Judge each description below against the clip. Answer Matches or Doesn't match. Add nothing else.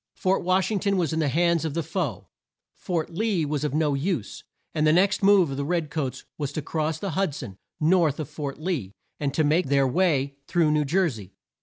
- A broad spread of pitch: Doesn't match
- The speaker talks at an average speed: Doesn't match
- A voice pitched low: Doesn't match